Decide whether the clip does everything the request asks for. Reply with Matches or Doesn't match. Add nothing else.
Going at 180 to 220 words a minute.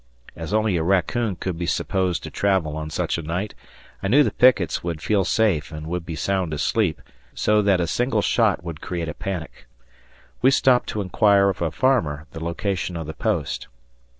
Matches